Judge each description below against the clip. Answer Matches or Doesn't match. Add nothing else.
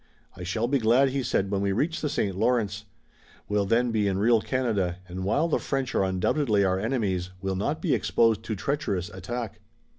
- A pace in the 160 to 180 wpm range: Doesn't match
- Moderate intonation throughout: Matches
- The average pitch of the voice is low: Matches